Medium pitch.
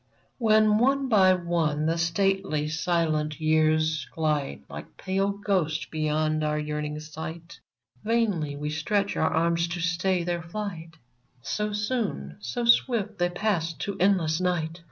Yes: medium, 170 Hz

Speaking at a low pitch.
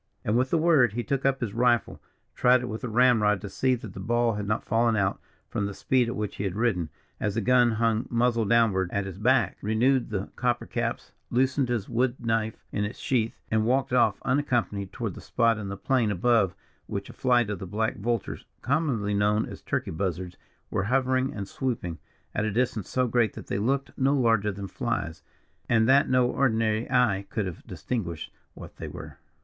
Yes: low, 115 Hz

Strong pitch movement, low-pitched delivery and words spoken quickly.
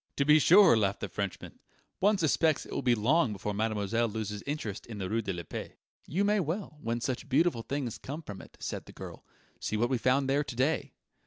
Yes: wide, 6.1 semitones; low, 125 Hz; fast, 225 wpm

